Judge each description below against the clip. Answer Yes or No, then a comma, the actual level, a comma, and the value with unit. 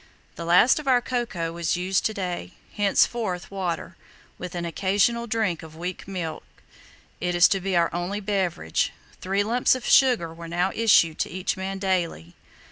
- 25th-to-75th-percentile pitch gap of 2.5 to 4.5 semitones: Yes, average, 3.3 semitones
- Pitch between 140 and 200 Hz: Yes, medium, 185 Hz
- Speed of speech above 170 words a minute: No, average, 165 wpm